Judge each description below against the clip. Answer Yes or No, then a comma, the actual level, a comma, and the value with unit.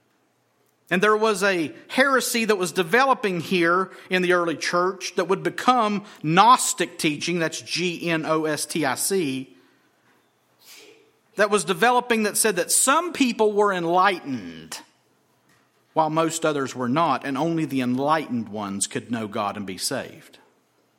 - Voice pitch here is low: No, medium, 185 Hz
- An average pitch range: No, wide, 5.7 semitones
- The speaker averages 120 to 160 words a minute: Yes, average, 150 wpm